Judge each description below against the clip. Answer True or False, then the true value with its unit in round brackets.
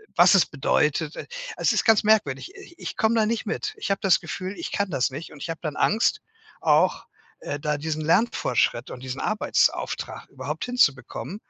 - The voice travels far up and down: True (6.9 semitones)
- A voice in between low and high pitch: True (175 Hz)